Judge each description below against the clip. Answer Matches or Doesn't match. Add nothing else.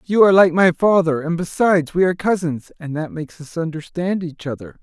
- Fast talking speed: Matches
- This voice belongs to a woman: Doesn't match